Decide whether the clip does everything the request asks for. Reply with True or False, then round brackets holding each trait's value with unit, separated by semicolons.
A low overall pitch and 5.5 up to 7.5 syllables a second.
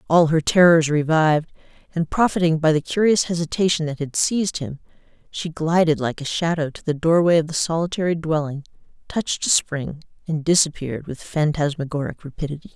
False (160 Hz; 5.6 syllables/s)